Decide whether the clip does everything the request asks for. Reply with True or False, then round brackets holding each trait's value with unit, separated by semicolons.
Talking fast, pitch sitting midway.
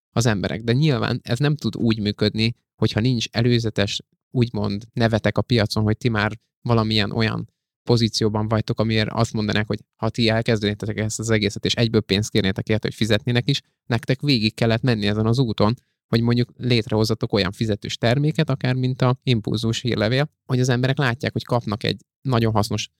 False (175 wpm; 115 Hz)